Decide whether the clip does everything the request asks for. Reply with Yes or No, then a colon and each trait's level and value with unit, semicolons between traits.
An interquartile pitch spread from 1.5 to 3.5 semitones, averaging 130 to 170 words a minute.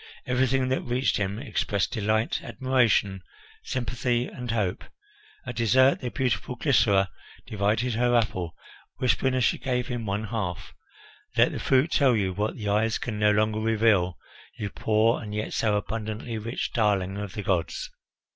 Yes: average, 3.1 semitones; average, 155 wpm